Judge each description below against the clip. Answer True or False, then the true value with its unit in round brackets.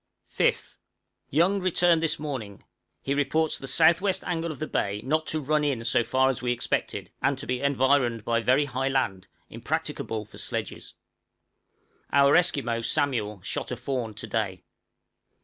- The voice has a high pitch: False (135 Hz)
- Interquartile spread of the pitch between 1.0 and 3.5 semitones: False (4.8 semitones)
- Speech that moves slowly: False (165 wpm)